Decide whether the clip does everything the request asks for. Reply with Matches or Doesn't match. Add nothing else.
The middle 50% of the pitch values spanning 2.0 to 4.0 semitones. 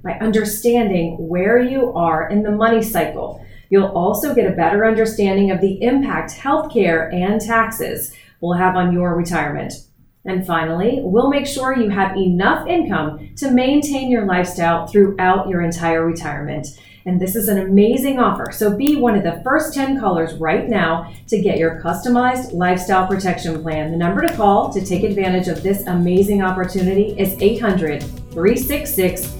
Doesn't match